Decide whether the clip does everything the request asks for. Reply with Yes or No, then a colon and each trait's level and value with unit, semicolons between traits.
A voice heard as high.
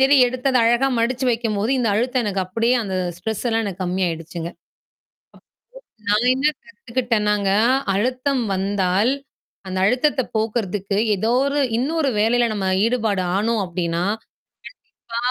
Yes: high, 225 Hz